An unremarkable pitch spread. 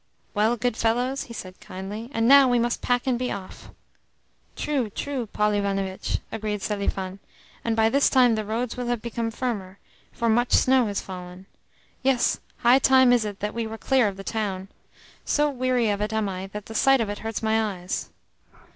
Yes: average, 3.3 semitones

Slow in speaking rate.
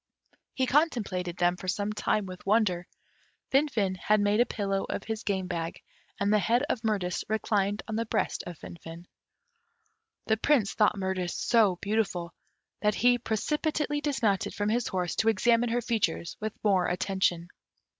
No: average, 160 wpm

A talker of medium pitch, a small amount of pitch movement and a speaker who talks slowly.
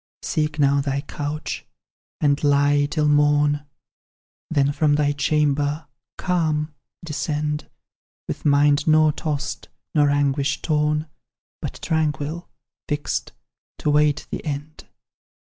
Yes: medium, 150 Hz; narrow, 1.0 semitones; slow, 110 wpm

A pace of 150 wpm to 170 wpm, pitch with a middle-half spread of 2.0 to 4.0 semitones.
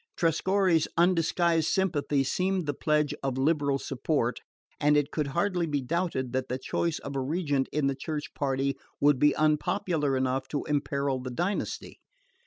Yes: average, 160 wpm; average, 3.6 semitones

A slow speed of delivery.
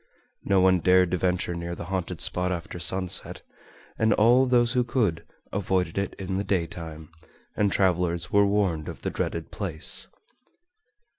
No: average, 155 wpm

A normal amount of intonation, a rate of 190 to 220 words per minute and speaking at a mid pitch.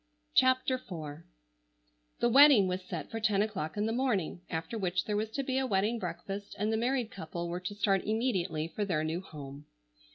No: average, 4.6 semitones; average, 195 wpm; high, 200 Hz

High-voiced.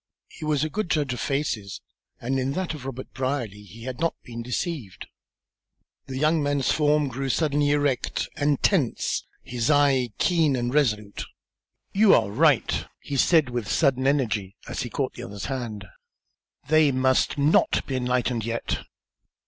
No: low, 135 Hz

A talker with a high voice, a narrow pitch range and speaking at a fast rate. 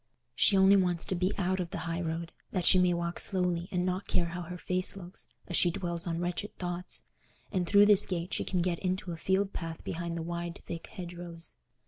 No: medium, 175 Hz; narrow, 1.4 semitones; fast, 220 wpm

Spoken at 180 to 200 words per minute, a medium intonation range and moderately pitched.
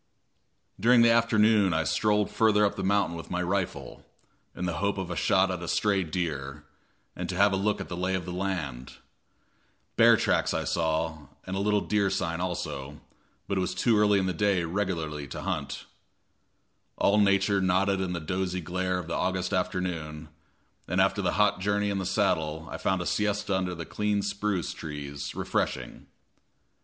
No: average, 185 wpm; average, 3.3 semitones; very low, 95 Hz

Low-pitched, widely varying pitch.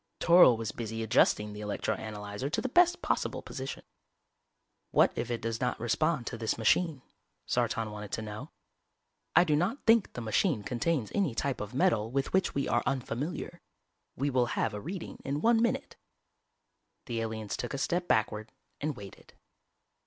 Yes: low, 125 Hz; wide, 6.5 semitones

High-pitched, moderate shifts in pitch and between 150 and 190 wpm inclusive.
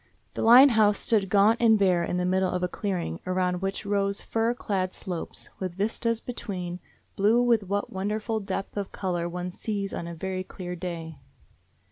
Yes: high, 195 Hz; average, 3.0 semitones; average, 180 wpm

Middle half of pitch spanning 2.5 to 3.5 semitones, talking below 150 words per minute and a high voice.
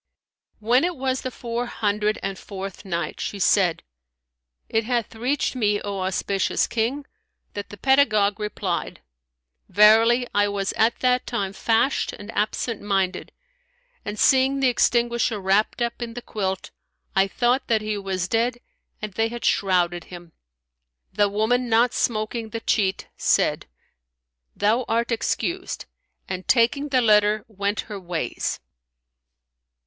Yes: average, 3.1 semitones; average, 140 wpm; high, 215 Hz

